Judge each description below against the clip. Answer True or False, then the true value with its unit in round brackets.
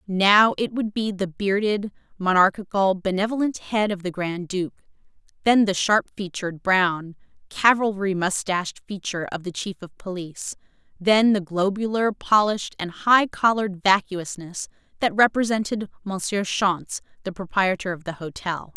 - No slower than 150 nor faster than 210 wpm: False (140 wpm)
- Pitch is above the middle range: True (195 Hz)